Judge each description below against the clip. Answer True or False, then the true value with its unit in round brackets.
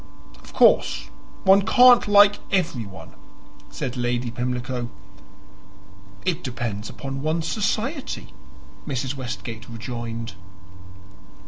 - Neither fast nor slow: False (90 wpm)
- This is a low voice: True (130 Hz)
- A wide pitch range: True (7.9 semitones)